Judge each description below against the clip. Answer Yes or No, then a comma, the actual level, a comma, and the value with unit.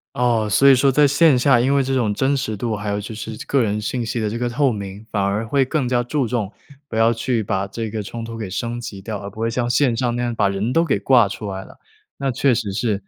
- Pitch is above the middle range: No, low, 115 Hz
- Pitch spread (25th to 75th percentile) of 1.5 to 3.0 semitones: No, average, 3.4 semitones